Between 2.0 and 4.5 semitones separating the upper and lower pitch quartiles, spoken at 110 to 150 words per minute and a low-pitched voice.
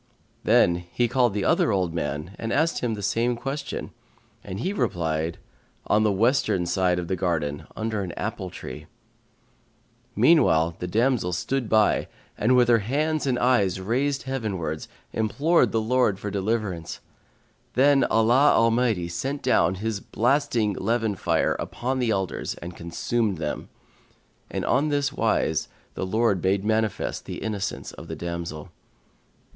No: average, 5.3 semitones; average, 145 wpm; low, 110 Hz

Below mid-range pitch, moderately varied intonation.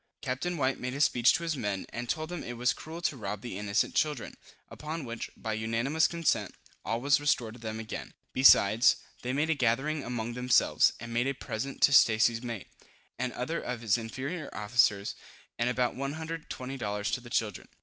Yes: low, 125 Hz; average, 3.9 semitones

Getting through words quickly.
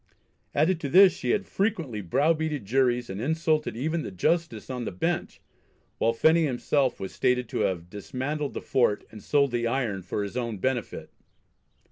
No: average, 170 wpm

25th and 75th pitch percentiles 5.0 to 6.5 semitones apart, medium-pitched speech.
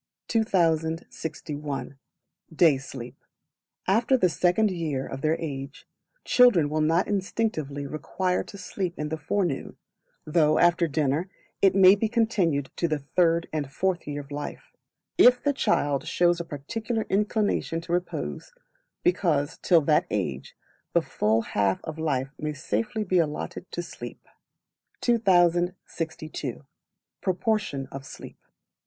No: average, 4.6 semitones; medium, 165 Hz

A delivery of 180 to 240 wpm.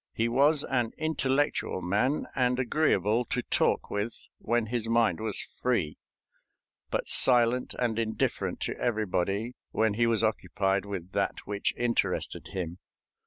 No: slow, 135 wpm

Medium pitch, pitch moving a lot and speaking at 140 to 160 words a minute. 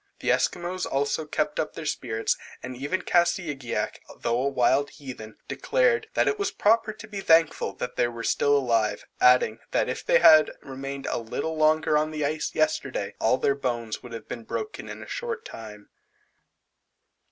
No: medium, 145 Hz; wide, 5.9 semitones; average, 175 wpm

